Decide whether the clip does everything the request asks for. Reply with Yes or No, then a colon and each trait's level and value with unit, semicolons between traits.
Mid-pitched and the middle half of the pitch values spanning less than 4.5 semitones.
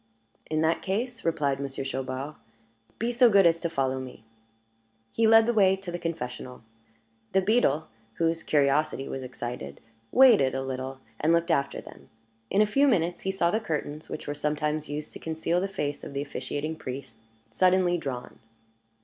No: medium, 155 Hz; wide, 5.6 semitones